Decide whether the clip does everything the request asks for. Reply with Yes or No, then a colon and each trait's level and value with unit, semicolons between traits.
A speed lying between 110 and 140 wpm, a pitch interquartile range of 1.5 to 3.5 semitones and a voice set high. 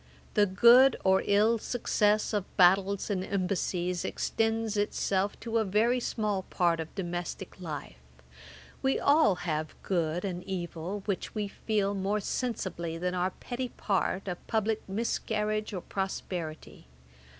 Yes: slow, 135 wpm; average, 3.0 semitones; high, 195 Hz